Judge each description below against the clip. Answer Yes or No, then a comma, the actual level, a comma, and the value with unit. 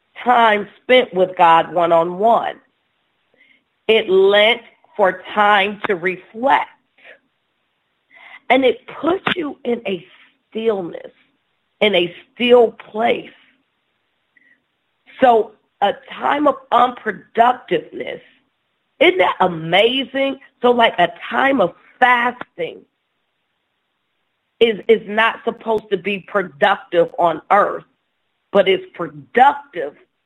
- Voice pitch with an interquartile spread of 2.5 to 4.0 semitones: No, average, 4.7 semitones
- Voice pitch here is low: No, high, 220 Hz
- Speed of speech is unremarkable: No, slow, 95 wpm